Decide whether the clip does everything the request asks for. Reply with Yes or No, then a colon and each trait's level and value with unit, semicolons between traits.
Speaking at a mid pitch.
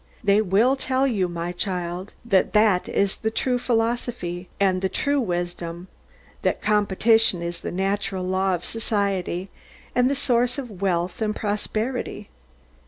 No: high, 200 Hz